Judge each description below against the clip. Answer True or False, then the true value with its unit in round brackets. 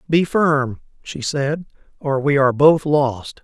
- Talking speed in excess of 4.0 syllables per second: False (3.7 syllables/s)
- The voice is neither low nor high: True (145 Hz)